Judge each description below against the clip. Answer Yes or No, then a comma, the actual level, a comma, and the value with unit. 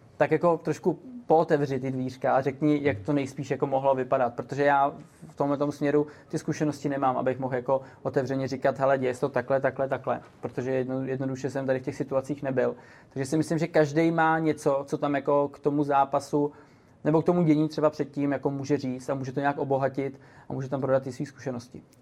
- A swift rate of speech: Yes, fast, 210 wpm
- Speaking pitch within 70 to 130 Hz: No, medium, 140 Hz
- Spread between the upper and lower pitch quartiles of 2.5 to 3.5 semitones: No, narrow, 1.9 semitones